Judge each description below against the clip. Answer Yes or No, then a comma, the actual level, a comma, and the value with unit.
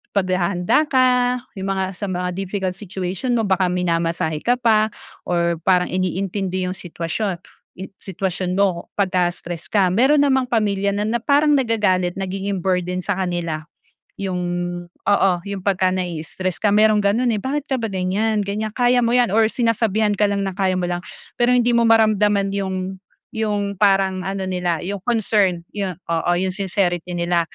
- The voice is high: Yes, high, 195 Hz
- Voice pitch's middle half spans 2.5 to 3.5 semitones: Yes, average, 3.1 semitones